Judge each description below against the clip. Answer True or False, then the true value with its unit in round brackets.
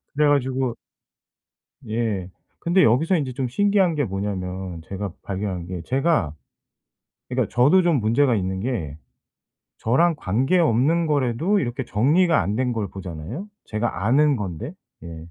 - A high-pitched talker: False (120 Hz)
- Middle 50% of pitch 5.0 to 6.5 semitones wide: False (7.4 semitones)